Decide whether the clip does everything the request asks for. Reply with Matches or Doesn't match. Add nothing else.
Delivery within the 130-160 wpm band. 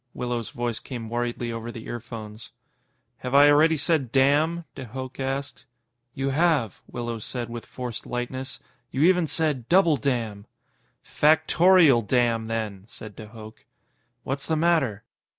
Matches